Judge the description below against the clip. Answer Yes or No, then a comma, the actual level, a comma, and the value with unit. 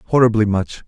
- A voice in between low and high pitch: No, low, 110 Hz